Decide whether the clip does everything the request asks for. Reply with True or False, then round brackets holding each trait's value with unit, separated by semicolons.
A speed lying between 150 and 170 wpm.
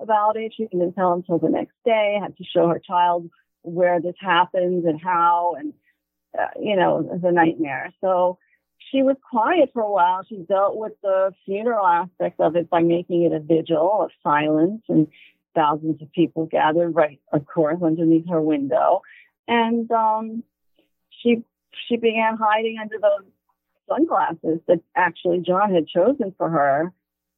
True (160 wpm)